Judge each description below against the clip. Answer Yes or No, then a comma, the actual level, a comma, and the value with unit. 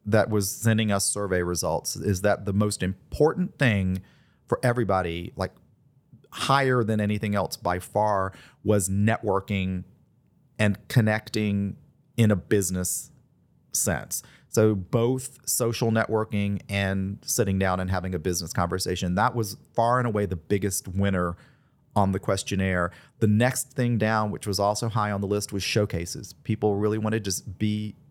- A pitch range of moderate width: Yes, average, 3.2 semitones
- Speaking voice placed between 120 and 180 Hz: No, low, 105 Hz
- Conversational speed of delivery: Yes, average, 150 wpm